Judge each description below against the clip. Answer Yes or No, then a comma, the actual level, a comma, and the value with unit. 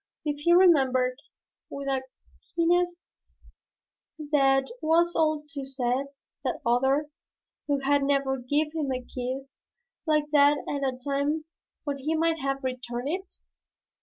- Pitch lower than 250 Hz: No, very high, 280 Hz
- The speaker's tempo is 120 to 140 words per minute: Yes, slow, 135 wpm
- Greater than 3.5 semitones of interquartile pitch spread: No, narrow, 2.5 semitones